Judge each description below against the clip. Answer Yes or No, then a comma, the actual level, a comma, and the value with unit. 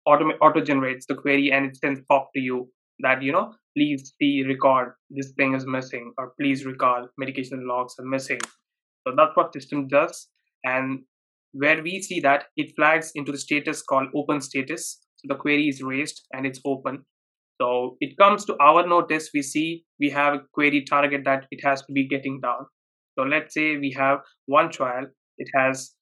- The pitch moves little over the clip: Yes, narrow, 1.8 semitones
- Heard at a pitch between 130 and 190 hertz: Yes, medium, 140 Hz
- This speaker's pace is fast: No, average, 190 wpm